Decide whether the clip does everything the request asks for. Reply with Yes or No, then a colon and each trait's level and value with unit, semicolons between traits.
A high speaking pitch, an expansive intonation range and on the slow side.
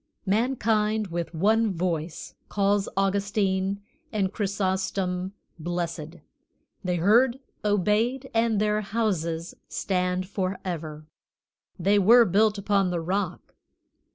No: high, 195 Hz; average, 2.7 semitones; slow, 100 wpm